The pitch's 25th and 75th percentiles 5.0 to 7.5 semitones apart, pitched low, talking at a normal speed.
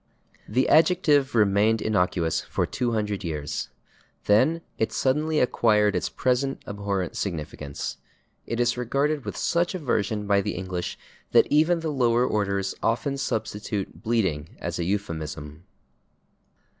No: wide, 5.5 semitones; low, 110 Hz; slow, 125 wpm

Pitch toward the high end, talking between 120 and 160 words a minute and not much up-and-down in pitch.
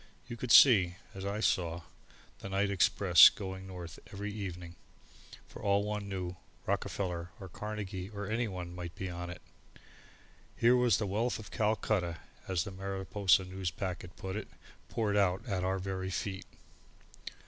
No: very low, 95 Hz; average, 150 wpm; narrow, 2.3 semitones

